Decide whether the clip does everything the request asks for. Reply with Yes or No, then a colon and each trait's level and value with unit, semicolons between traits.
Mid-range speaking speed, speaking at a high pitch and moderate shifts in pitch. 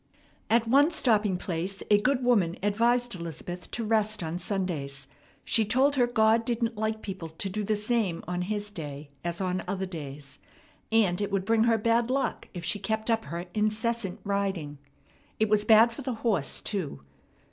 Yes: average, 180 wpm; high, 210 Hz; average, 4.2 semitones